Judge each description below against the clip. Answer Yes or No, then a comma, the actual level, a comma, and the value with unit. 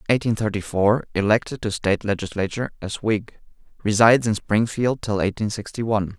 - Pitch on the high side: No, low, 105 Hz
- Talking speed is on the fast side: No, average, 145 wpm